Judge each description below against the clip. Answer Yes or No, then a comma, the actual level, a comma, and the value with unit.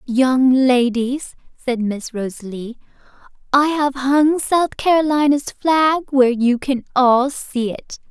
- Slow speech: Yes, slow, 125 wpm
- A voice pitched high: Yes, very high, 265 Hz